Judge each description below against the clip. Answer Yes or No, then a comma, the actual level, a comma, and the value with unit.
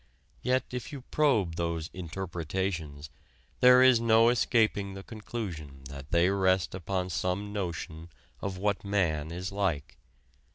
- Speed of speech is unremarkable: No, slow, 130 wpm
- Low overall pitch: Yes, very low, 95 Hz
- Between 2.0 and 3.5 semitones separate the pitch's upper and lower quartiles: No, average, 4.0 semitones